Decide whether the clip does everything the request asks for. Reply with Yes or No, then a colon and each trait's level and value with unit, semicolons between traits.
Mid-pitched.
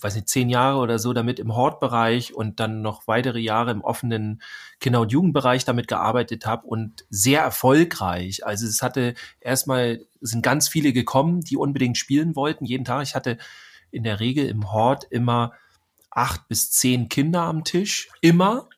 No: low, 125 Hz